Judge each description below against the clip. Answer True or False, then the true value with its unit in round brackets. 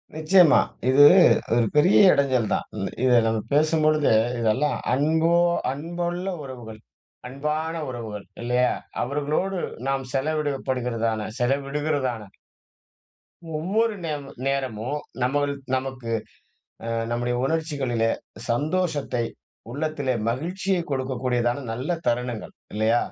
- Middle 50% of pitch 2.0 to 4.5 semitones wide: True (4.0 semitones)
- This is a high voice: False (135 Hz)